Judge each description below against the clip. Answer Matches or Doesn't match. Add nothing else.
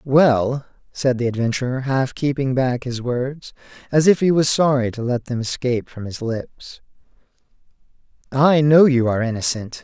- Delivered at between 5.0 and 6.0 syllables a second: Doesn't match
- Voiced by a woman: Doesn't match